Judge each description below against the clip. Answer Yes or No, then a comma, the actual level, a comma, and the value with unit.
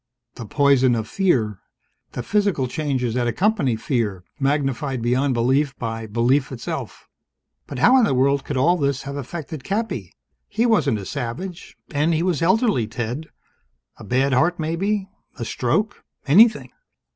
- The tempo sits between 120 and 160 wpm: Yes, average, 150 wpm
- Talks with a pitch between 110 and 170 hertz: Yes, medium, 140 Hz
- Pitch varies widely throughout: Yes, wide, 5.9 semitones